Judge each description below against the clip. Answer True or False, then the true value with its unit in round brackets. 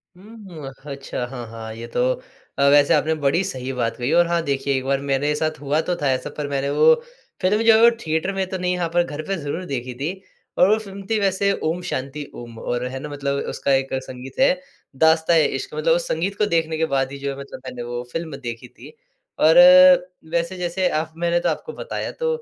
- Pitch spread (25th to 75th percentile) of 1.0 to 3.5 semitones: False (5.2 semitones)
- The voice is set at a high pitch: False (155 Hz)